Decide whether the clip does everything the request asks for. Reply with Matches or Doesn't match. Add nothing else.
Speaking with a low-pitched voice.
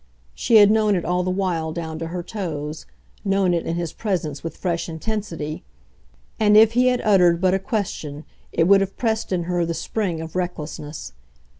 Doesn't match